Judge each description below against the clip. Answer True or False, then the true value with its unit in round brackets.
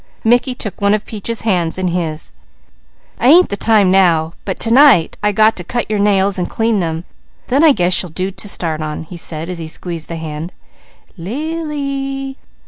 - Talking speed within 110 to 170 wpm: False (195 wpm)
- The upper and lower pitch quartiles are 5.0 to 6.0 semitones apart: True (5.6 semitones)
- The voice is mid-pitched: False (195 Hz)